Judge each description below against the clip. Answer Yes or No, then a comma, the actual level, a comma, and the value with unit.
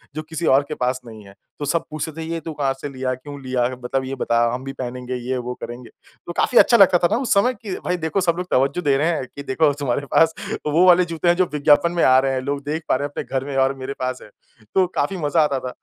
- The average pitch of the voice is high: No, medium, 145 Hz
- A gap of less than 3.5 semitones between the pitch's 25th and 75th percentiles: No, average, 4.2 semitones